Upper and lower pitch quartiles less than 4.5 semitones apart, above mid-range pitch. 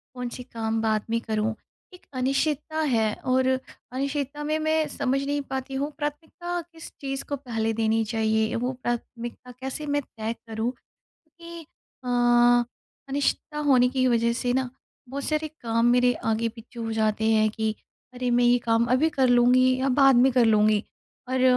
Yes: average, 3.2 semitones; very high, 250 Hz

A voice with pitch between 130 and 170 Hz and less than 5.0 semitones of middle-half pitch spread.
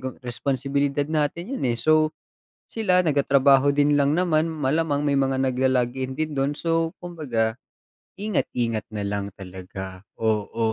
Yes: medium, 140 Hz; average, 4.5 semitones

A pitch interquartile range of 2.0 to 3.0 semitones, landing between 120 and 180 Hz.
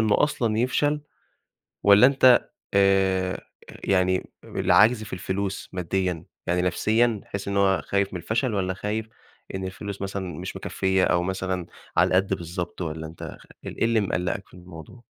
No: narrow, 2.6 semitones; very low, 95 Hz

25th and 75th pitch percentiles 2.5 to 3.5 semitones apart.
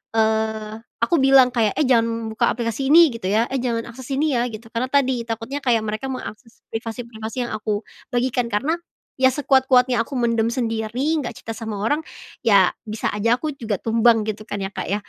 Yes: average, 2.8 semitones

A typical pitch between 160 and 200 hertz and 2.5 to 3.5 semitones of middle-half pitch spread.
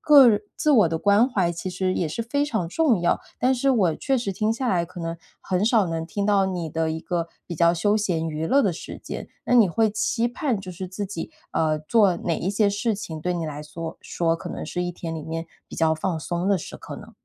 No: medium, 185 Hz; average, 4.6 semitones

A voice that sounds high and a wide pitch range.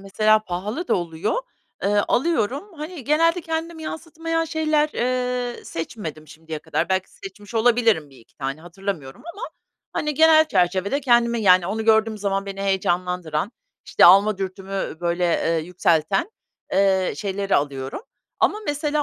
Yes: high, 200 Hz; wide, 8.3 semitones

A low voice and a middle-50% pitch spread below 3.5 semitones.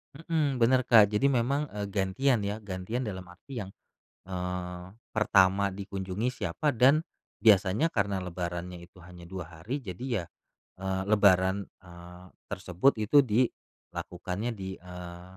No: very low, 95 Hz; average, 4.2 semitones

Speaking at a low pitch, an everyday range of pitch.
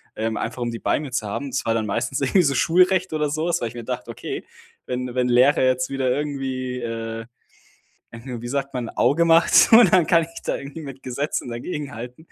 Yes: low, 130 Hz; average, 3.7 semitones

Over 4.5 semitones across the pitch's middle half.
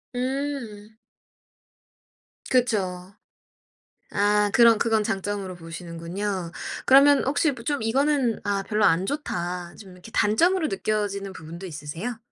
Yes: average, 5.3 semitones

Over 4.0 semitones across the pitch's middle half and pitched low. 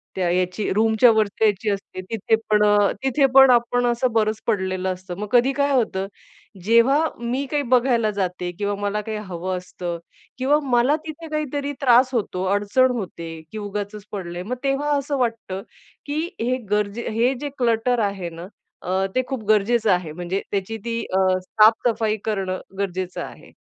No: average, 4.5 semitones; high, 215 Hz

